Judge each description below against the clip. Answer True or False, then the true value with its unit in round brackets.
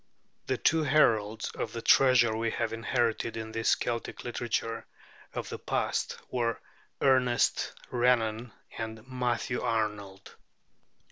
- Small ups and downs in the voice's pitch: True (1.9 semitones)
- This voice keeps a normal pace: False (120 wpm)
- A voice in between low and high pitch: False (115 Hz)